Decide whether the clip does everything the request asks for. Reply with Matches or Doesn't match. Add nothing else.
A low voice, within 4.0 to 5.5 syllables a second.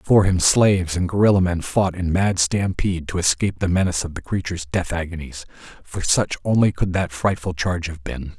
Doesn't match